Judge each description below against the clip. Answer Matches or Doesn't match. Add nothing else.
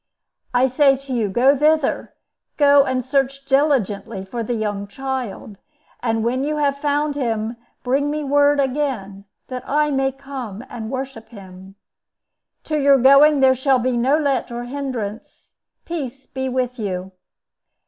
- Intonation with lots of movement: Doesn't match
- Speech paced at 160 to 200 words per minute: Doesn't match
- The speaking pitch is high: Matches